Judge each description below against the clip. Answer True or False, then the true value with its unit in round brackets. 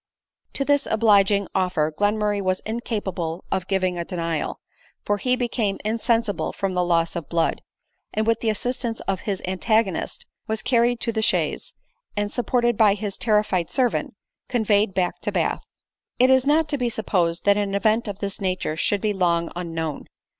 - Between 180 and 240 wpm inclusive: False (170 wpm)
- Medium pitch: False (205 Hz)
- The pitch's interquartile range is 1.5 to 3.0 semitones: False (3.8 semitones)